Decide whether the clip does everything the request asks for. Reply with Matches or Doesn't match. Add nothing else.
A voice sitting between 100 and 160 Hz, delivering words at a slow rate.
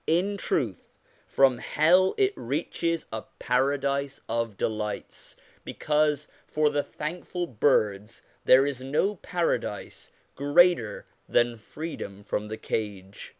Matches